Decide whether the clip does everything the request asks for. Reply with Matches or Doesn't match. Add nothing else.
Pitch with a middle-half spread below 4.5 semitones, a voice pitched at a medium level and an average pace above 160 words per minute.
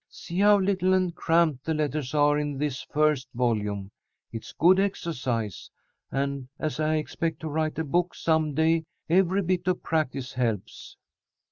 Doesn't match